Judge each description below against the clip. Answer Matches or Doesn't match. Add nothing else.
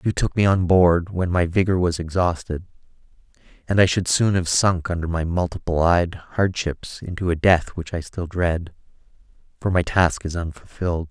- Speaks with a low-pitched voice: Matches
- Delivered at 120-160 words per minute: Doesn't match